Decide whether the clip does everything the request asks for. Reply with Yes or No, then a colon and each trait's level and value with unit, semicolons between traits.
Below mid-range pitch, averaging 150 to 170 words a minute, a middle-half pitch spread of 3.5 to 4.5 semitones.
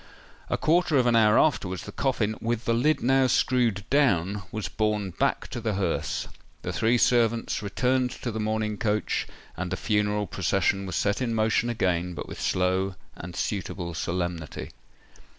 Yes: low, 105 Hz; average, 160 wpm; average, 4.0 semitones